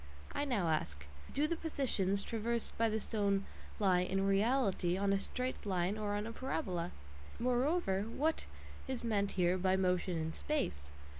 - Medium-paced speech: Yes, average, 160 wpm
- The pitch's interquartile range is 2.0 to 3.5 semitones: No, average, 4.7 semitones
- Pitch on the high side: Yes, high, 200 Hz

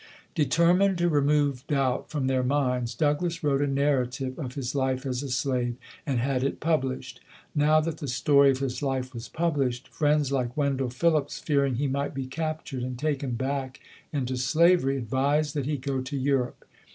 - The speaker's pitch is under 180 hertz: Yes, low, 135 Hz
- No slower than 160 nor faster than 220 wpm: Yes, average, 175 wpm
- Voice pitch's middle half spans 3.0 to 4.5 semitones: No, narrow, 2.4 semitones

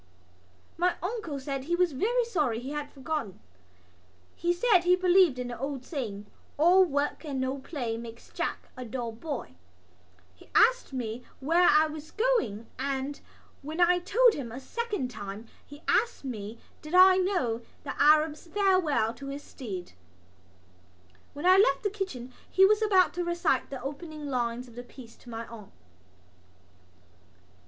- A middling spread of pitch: No, wide, 6.4 semitones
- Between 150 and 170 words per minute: Yes, average, 165 wpm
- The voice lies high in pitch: Yes, very high, 290 Hz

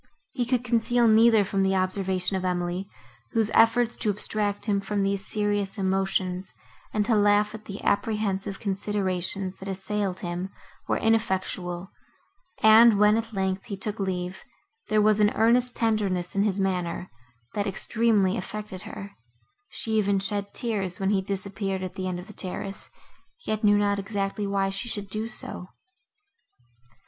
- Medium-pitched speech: No, high, 200 Hz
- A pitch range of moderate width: No, narrow, 2.0 semitones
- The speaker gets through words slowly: No, average, 155 wpm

